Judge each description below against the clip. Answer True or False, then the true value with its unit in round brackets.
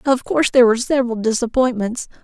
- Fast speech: False (160 wpm)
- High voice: True (245 Hz)